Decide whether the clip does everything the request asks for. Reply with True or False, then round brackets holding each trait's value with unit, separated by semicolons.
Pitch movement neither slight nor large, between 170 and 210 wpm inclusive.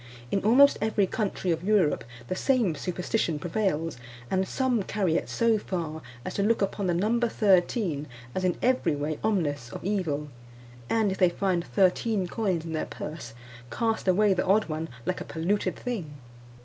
True (4.7 semitones; 175 wpm)